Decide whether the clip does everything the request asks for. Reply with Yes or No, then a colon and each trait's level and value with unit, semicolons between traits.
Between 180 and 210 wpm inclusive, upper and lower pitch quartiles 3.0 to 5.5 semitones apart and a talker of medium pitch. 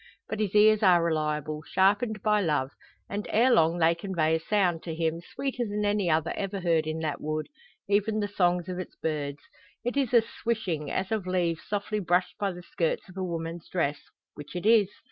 Yes: average, 200 wpm; average, 4.3 semitones; medium, 180 Hz